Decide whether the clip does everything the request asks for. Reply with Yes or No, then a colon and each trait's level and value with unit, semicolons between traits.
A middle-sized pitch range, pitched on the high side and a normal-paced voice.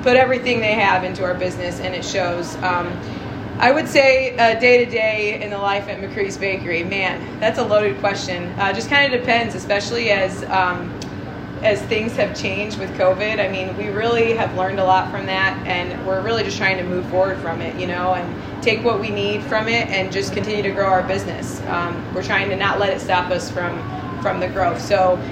No: average, 3.6 semitones; high, 210 Hz; fast, 220 wpm